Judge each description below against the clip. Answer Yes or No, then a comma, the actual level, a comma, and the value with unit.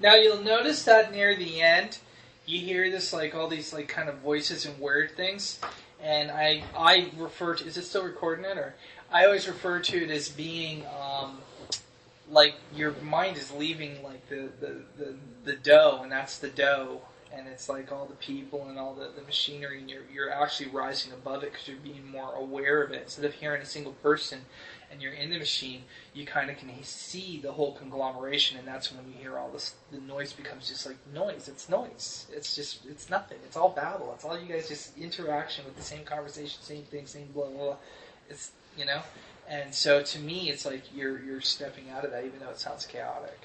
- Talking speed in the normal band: No, fast, 215 wpm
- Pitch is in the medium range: Yes, medium, 145 Hz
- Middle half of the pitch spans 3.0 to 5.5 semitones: No, narrow, 2.5 semitones